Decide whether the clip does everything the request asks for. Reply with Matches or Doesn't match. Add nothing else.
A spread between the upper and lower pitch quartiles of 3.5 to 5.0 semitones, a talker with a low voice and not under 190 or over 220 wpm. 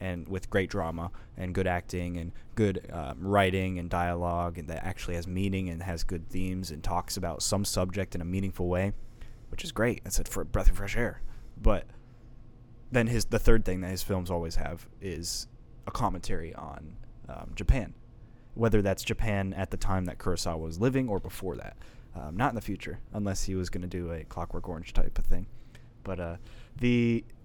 Matches